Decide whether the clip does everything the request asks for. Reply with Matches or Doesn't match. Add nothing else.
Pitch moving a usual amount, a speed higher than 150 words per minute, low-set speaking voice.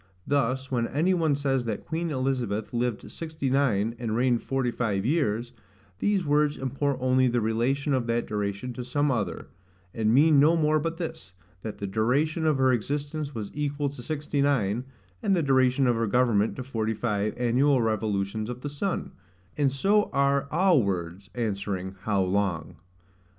Matches